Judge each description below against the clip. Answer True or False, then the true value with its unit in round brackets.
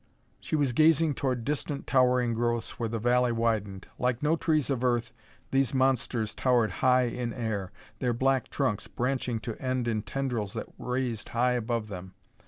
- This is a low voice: True (125 Hz)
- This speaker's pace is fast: False (170 wpm)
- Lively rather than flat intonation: False (2.4 semitones)